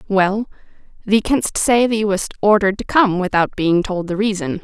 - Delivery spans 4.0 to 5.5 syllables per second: Yes, 4.8 syllables/s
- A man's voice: No, female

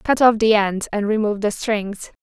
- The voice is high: Yes, high, 210 Hz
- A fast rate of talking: Yes, fast, 215 wpm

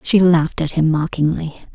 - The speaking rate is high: No, average, 170 wpm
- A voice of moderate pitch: Yes, medium, 160 Hz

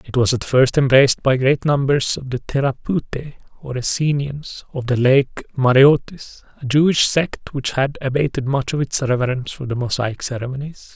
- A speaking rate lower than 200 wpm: Yes, average, 170 wpm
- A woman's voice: No, male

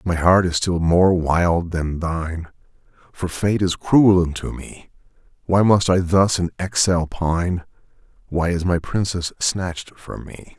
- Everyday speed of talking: Yes, average, 160 wpm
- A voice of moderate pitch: No, very low, 90 Hz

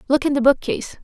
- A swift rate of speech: Yes, fast, 230 wpm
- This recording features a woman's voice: Yes, female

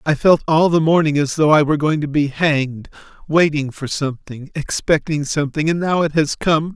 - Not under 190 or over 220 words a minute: Yes, fast, 205 wpm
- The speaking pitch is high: No, medium, 150 Hz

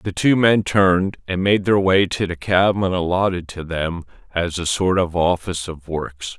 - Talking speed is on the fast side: No, average, 195 wpm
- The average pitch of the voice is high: No, very low, 90 Hz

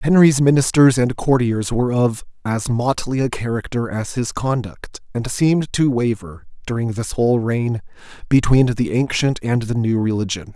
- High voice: No, low, 120 Hz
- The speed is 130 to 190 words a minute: Yes, average, 160 wpm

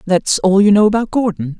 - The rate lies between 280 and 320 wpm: No, fast, 225 wpm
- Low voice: No, high, 200 Hz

